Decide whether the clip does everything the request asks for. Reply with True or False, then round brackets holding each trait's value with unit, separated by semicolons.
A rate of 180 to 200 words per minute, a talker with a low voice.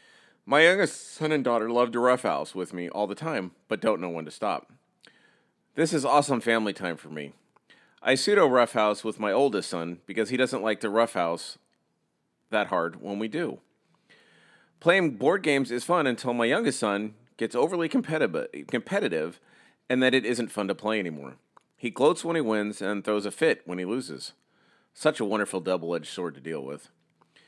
True (185 wpm; 110 Hz)